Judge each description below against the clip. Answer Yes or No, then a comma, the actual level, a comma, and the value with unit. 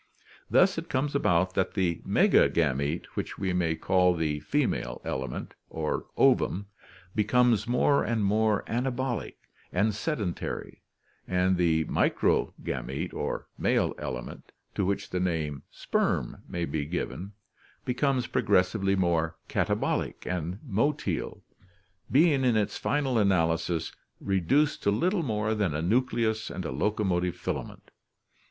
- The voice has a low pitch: Yes, very low, 95 Hz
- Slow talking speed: Yes, slow, 125 wpm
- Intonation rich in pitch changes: Yes, wide, 5.8 semitones